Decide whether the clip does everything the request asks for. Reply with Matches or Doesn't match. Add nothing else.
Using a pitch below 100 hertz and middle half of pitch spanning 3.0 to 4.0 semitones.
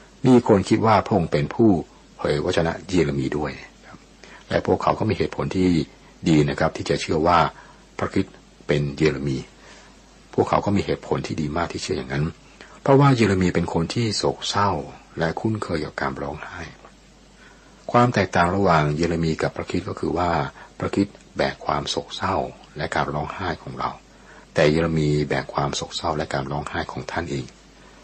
Doesn't match